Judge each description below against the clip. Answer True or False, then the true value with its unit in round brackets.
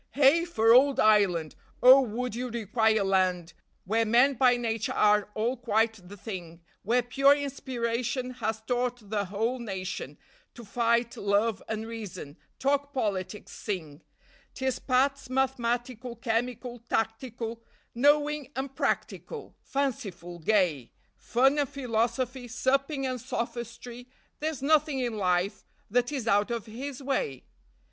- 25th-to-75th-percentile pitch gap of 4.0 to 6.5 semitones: False (3.6 semitones)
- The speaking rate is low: True (130 wpm)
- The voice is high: True (235 Hz)